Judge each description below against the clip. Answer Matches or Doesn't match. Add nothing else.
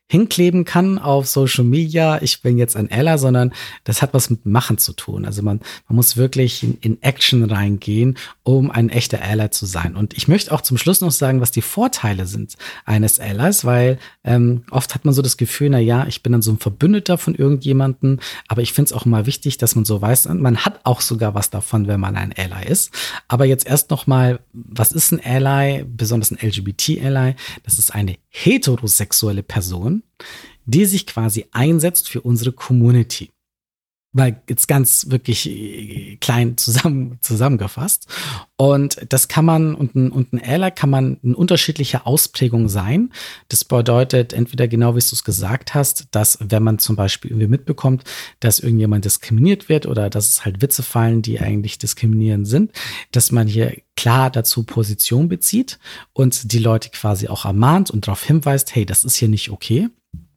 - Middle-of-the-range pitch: Doesn't match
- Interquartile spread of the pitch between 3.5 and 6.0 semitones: Matches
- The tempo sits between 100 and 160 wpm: Doesn't match